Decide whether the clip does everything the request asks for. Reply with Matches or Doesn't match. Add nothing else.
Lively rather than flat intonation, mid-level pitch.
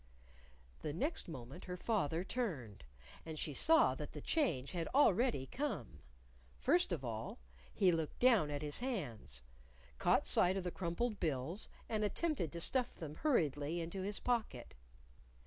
Matches